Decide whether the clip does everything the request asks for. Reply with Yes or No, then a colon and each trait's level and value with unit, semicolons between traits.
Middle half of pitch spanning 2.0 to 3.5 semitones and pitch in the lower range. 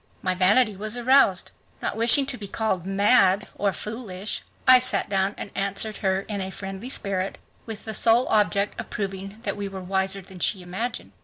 No: narrow, 2.6 semitones; high, 200 Hz